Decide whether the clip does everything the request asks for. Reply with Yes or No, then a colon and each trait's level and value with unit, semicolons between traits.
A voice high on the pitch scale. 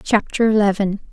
Yes: high, 205 Hz